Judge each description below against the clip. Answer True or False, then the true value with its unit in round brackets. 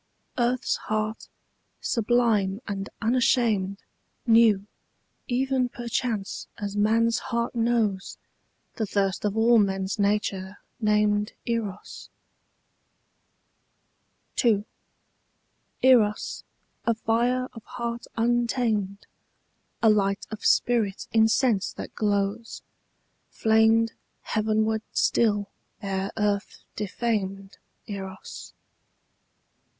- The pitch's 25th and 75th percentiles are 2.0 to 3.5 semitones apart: True (2.5 semitones)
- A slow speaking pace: True (85 wpm)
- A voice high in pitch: True (215 Hz)